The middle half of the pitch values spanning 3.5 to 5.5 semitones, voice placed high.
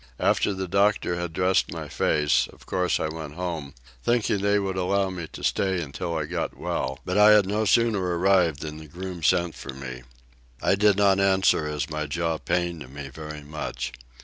No: average, 4.0 semitones; very low, 85 Hz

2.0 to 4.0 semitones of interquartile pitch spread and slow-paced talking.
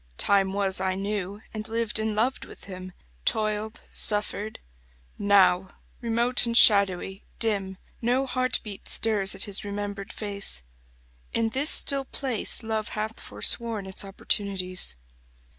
Yes: narrow, 2.5 semitones; slow, 125 wpm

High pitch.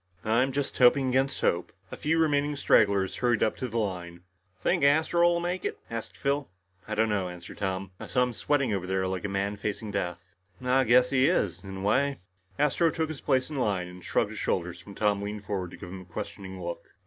No: low, 110 Hz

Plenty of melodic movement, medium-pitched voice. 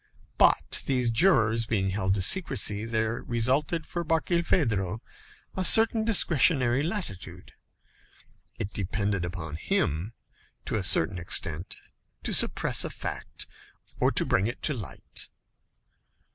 No: wide, 8.2 semitones; low, 115 Hz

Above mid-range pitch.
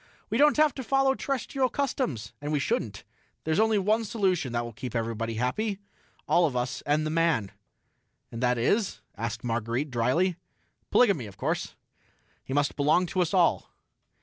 No: medium, 155 Hz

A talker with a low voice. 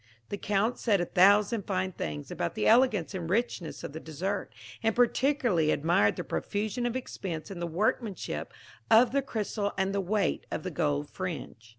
No: high, 195 Hz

